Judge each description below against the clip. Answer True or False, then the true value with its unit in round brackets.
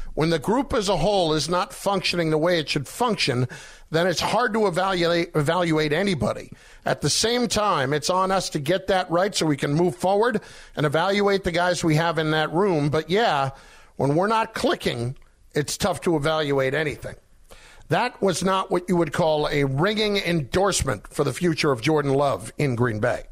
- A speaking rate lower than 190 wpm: False (195 wpm)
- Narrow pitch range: False (4.0 semitones)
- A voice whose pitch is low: False (170 Hz)